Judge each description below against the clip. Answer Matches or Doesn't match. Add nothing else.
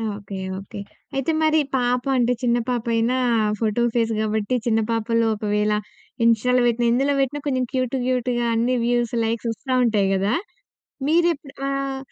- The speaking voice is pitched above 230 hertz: Matches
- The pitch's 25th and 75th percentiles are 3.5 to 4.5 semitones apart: Doesn't match